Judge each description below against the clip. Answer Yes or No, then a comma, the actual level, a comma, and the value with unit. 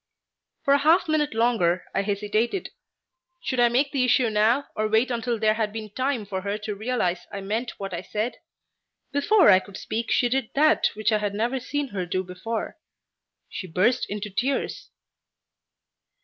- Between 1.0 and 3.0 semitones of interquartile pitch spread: No, average, 3.9 semitones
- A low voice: No, high, 220 Hz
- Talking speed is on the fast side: No, average, 175 wpm